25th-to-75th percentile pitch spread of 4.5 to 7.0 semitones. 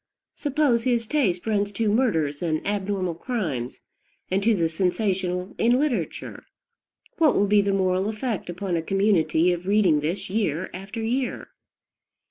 No: average, 4.1 semitones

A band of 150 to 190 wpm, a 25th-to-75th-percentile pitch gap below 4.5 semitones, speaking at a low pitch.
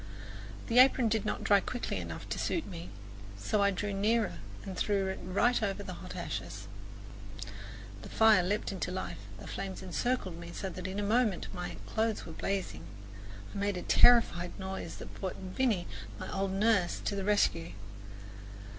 No: average, 170 wpm; average, 2.9 semitones; high, 195 Hz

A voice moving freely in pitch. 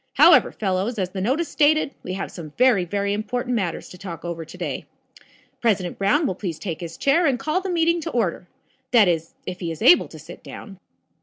Yes: wide, 6.5 semitones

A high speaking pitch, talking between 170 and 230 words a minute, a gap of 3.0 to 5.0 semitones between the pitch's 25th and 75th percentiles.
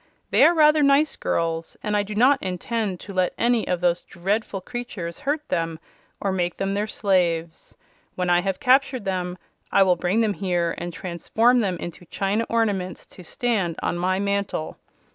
Yes: high, 195 Hz; average, 180 wpm; average, 4.4 semitones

